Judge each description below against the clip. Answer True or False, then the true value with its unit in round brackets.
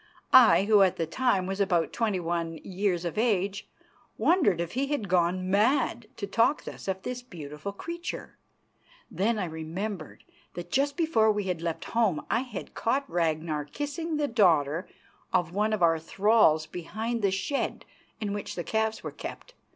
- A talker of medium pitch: False (200 Hz)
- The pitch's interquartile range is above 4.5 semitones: True (5.1 semitones)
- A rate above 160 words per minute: True (170 wpm)